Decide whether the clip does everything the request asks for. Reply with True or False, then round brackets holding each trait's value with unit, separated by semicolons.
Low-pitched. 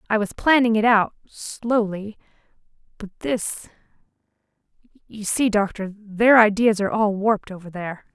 False (210 Hz)